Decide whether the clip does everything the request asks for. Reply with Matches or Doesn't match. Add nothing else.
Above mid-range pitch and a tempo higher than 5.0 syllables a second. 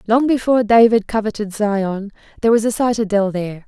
Matches